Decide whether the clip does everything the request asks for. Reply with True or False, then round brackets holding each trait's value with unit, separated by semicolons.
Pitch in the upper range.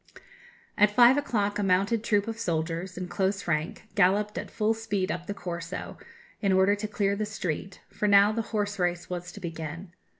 True (200 Hz)